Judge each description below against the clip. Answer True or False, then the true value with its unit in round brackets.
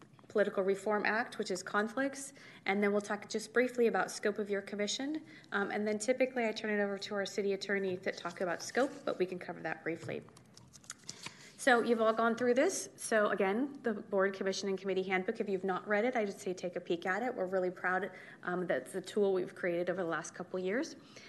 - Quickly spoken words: True (230 wpm)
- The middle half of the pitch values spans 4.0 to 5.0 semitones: False (3.3 semitones)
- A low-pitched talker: False (200 Hz)